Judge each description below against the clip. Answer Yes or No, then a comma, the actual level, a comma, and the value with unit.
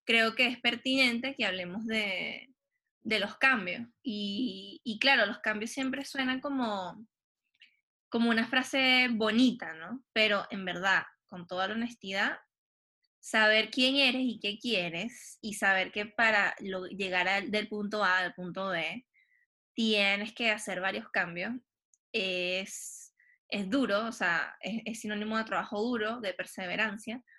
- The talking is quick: No, average, 145 wpm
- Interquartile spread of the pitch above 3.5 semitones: Yes, average, 4.1 semitones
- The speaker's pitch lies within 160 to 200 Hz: No, high, 220 Hz